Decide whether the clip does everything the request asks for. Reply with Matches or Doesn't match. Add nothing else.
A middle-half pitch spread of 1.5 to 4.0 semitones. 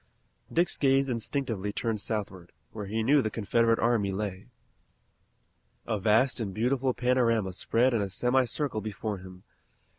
Matches